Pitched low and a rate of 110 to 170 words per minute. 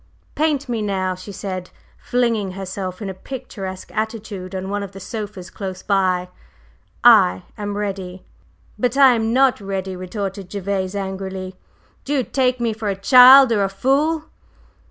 No: high, 200 Hz; average, 155 wpm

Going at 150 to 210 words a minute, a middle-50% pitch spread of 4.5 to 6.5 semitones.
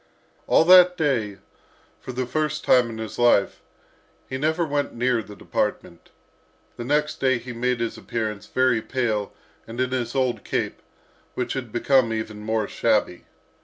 No: average, 160 wpm; average, 3.1 semitones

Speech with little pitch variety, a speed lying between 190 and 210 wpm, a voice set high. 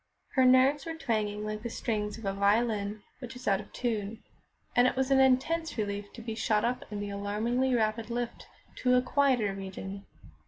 No: average, 3.5 semitones; average, 195 wpm; high, 225 Hz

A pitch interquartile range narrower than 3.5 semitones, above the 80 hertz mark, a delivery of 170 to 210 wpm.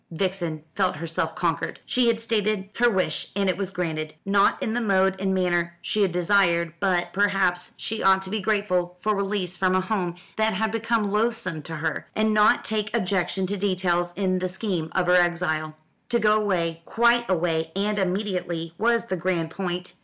Yes: average, 3.1 semitones; high, 190 Hz; average, 190 wpm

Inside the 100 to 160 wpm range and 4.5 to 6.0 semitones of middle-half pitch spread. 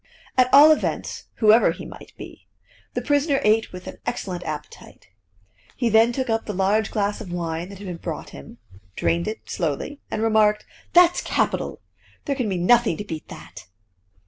No: average, 175 wpm; average, 5.1 semitones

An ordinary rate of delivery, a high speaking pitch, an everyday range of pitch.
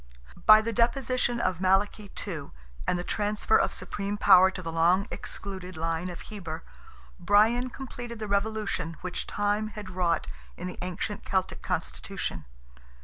Yes: average, 145 wpm; high, 200 Hz; average, 3.1 semitones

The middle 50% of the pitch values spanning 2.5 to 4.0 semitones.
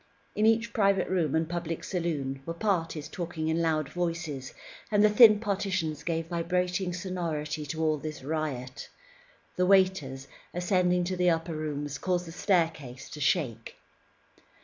Yes: average, 3.0 semitones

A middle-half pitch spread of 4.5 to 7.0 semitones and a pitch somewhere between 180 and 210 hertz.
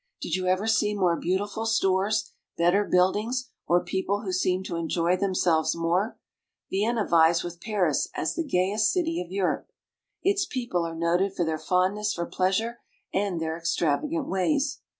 No: average, 3.7 semitones; high, 190 Hz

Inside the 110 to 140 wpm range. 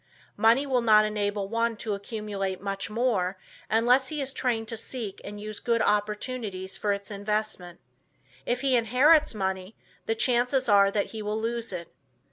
No: average, 165 wpm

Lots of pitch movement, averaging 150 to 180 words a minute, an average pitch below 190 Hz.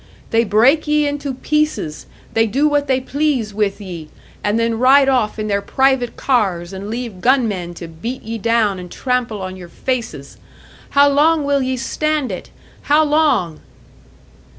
No: wide, 5.8 semitones; average, 165 wpm; high, 235 Hz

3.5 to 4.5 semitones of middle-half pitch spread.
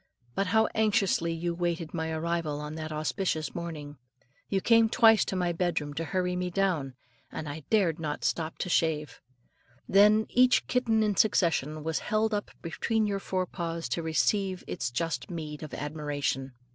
Yes: average, 4.2 semitones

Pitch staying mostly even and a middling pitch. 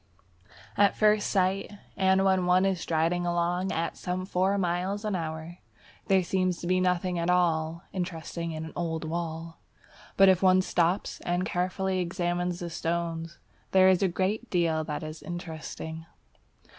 Yes: narrow, 2.0 semitones; medium, 175 Hz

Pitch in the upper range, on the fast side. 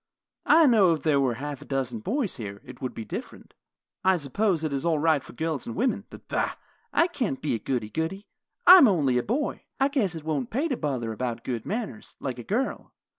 No: medium, 155 Hz; fast, 230 wpm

